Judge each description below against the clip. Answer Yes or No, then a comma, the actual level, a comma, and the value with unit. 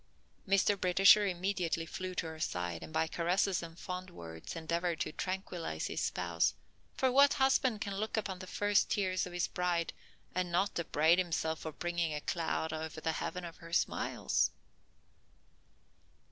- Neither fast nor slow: Yes, average, 160 wpm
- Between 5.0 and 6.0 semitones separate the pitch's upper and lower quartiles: No, average, 2.9 semitones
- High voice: No, medium, 175 Hz